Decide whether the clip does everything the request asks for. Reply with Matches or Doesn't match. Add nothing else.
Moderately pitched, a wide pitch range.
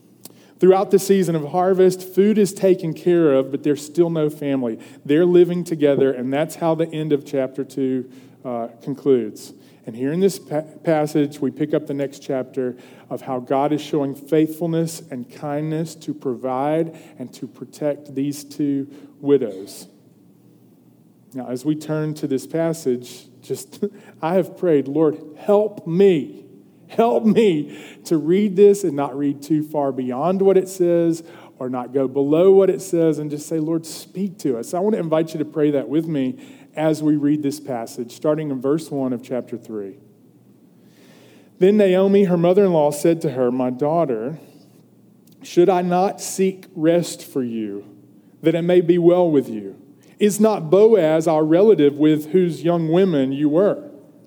Doesn't match